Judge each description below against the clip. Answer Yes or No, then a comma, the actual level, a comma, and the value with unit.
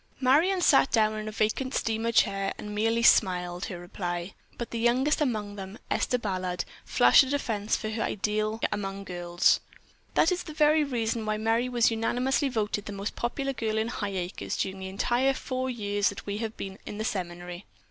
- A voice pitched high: Yes, high, 215 Hz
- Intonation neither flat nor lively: Yes, average, 3.8 semitones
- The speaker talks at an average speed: Yes, average, 185 wpm